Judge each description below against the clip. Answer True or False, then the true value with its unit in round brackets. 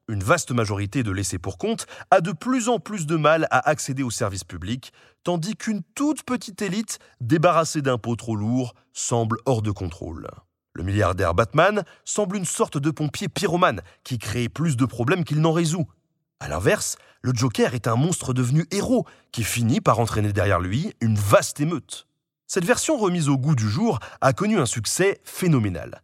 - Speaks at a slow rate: False (180 wpm)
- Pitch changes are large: True (7.8 semitones)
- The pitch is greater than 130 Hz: True (140 Hz)